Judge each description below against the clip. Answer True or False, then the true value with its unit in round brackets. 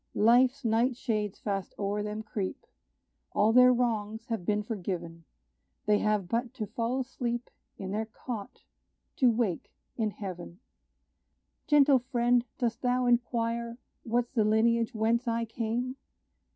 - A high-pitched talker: True (230 Hz)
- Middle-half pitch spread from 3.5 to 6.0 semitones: False (2.5 semitones)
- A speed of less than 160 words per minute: True (135 wpm)